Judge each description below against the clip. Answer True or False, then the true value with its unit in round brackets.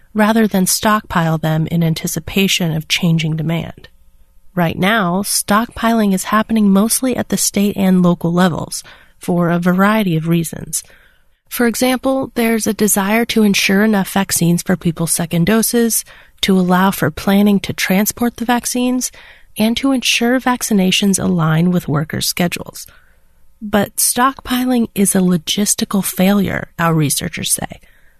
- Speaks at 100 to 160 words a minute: True (135 wpm)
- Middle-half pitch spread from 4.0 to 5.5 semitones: True (4.5 semitones)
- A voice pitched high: True (195 Hz)